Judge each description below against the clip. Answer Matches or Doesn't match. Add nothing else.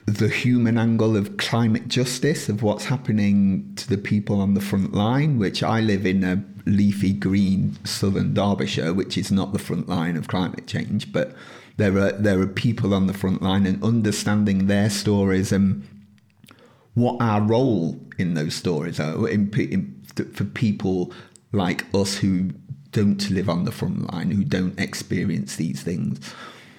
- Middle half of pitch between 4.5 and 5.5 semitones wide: Doesn't match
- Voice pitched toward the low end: Matches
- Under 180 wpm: Matches